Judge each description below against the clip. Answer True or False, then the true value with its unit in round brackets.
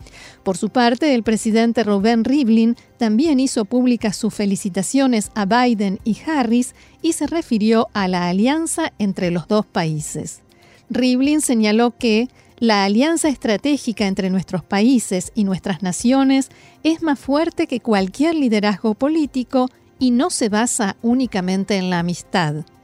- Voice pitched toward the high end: True (230 Hz)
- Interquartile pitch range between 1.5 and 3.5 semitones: False (4.5 semitones)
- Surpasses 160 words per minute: False (140 wpm)